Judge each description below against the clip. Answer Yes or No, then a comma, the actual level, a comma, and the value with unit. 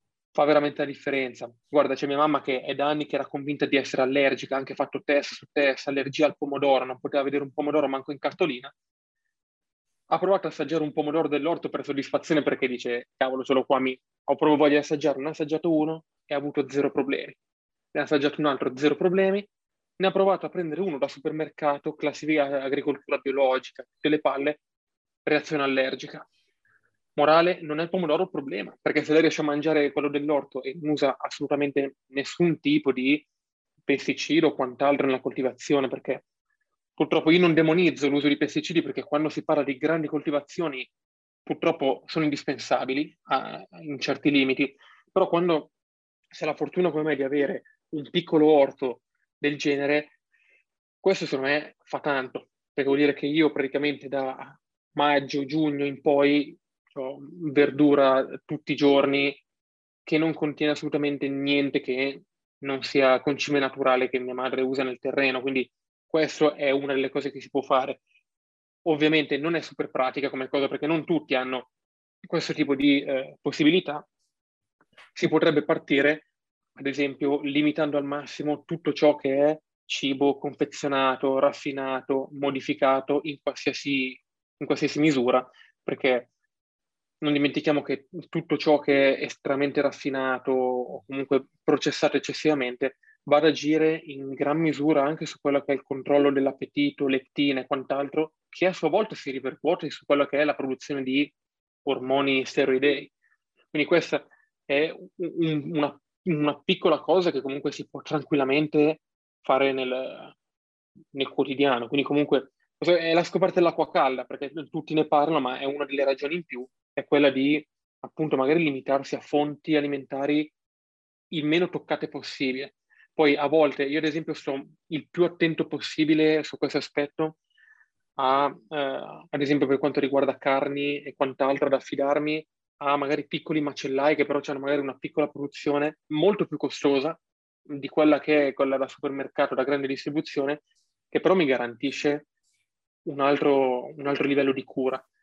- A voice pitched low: No, medium, 145 Hz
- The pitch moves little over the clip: Yes, narrow, 1.9 semitones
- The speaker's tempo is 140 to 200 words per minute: Yes, average, 160 wpm